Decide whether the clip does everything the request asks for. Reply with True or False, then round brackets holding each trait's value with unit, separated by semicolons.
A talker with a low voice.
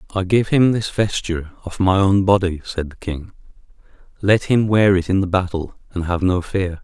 True (95 Hz)